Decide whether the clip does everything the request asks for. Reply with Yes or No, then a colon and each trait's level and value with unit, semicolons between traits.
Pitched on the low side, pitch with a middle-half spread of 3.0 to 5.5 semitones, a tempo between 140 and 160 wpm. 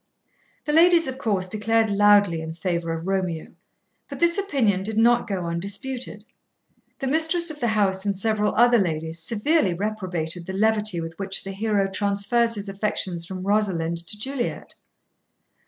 No: high, 205 Hz; average, 3.9 semitones; average, 155 wpm